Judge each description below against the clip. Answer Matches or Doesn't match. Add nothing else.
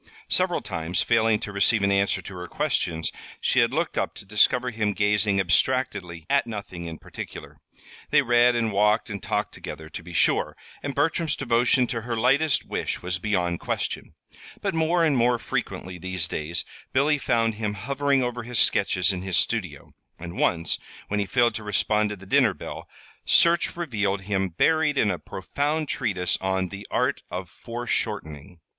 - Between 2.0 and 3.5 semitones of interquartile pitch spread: Doesn't match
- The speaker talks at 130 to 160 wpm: Doesn't match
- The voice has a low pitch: Matches